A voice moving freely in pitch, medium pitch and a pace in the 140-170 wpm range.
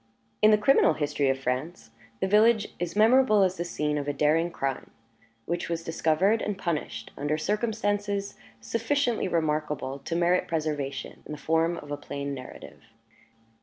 Yes: wide, 5.7 semitones; medium, 165 Hz; average, 160 wpm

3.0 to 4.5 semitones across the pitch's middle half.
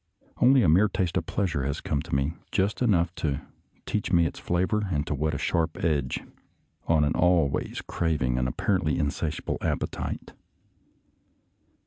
Yes: average, 4.2 semitones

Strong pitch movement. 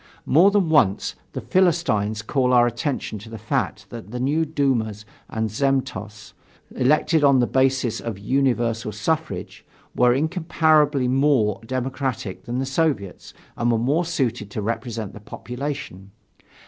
No: average, 4.6 semitones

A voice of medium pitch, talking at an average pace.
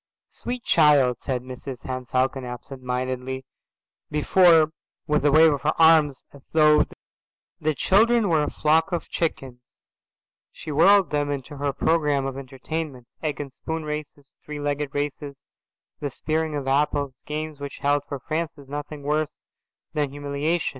Yes: medium, 145 Hz; average, 155 wpm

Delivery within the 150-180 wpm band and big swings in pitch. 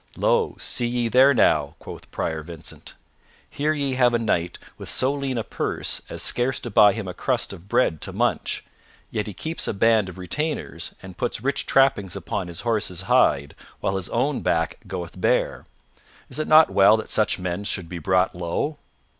No: average, 190 wpm; wide, 6.1 semitones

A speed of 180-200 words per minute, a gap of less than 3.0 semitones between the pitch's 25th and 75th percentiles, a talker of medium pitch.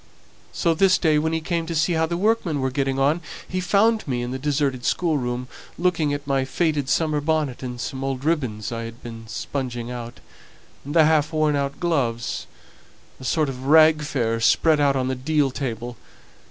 No: average, 185 wpm; average, 4.0 semitones; medium, 145 Hz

